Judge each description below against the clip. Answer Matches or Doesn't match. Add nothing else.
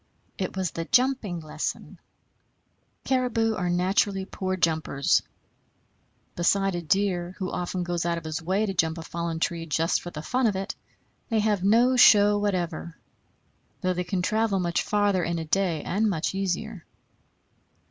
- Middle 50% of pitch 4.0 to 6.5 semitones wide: Doesn't match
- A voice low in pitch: Doesn't match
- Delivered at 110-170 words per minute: Matches